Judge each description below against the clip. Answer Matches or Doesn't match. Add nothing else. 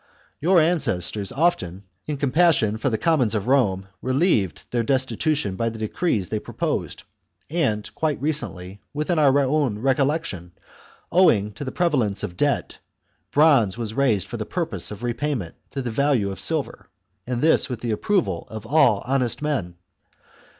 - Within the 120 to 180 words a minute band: Matches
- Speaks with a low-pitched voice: Matches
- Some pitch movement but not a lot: Doesn't match